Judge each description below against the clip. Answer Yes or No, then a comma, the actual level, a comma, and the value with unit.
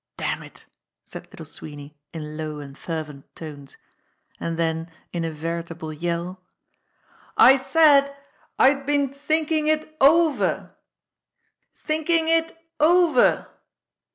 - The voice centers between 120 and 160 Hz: No, medium, 185 Hz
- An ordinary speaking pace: No, slow, 115 wpm